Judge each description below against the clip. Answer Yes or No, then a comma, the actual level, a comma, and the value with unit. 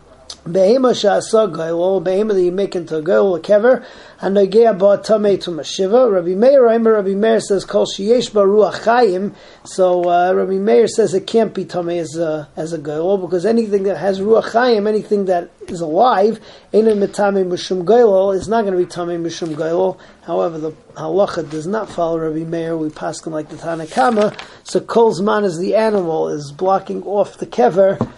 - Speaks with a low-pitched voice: No, high, 195 Hz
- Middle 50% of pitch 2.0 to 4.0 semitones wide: Yes, average, 3.5 semitones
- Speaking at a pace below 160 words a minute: No, average, 175 wpm